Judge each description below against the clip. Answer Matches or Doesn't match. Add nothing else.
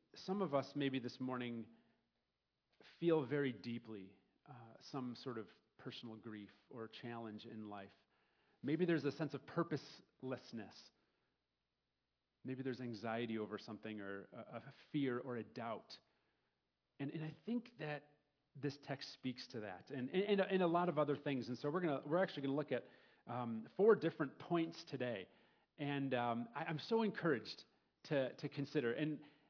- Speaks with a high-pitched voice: Doesn't match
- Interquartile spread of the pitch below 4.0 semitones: Doesn't match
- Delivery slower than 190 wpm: Matches